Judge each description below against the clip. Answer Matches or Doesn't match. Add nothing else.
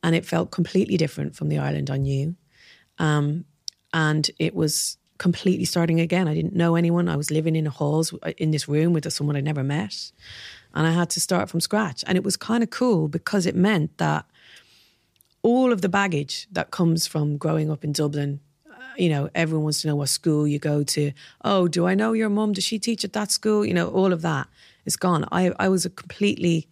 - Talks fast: Matches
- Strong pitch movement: Doesn't match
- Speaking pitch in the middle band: Matches